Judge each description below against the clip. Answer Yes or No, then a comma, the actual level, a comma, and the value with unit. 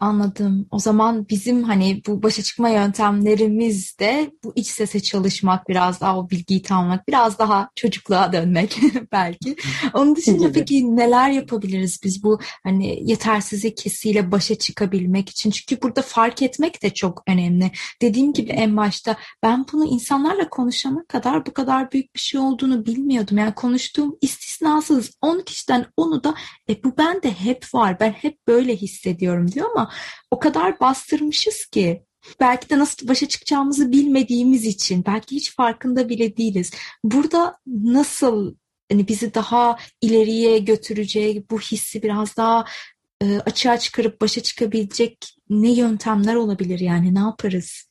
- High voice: Yes, high, 225 Hz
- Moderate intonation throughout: Yes, average, 4.4 semitones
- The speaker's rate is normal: No, fast, 145 wpm